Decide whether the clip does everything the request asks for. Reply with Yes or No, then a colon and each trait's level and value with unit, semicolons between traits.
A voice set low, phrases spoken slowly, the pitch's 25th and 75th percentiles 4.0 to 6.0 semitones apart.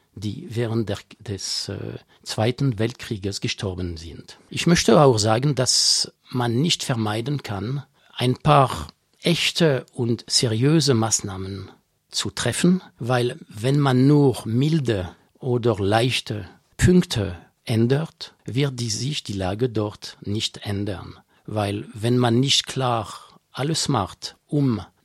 Yes: low, 120 Hz; slow, 120 wpm; average, 4.7 semitones